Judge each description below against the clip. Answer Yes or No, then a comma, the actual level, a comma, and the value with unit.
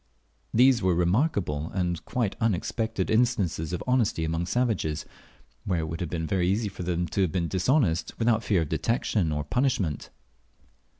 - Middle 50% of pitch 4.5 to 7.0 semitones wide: Yes, wide, 5.5 semitones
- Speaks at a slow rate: No, average, 165 wpm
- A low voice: Yes, very low, 95 Hz